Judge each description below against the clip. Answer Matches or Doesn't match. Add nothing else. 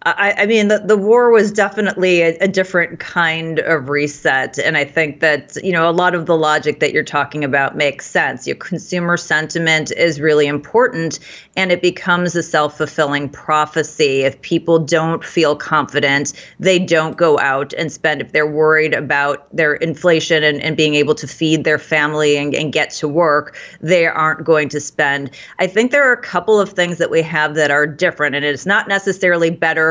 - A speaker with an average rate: Matches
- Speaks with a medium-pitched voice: Matches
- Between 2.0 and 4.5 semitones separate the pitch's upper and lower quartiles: Matches